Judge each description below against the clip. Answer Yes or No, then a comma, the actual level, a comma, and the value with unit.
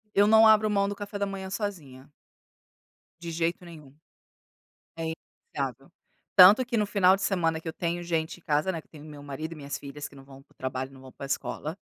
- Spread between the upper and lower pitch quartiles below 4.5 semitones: No, wide, 5.4 semitones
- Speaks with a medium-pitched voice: Yes, medium, 165 Hz